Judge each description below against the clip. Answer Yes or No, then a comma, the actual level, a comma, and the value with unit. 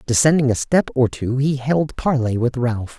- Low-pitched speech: Yes, low, 130 Hz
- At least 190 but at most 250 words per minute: Yes, average, 200 wpm